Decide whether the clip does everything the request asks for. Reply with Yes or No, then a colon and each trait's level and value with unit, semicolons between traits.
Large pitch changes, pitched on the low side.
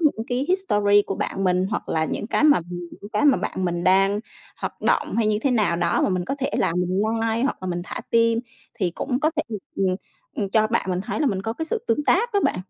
No: wide, 5.8 semitones; high, 210 Hz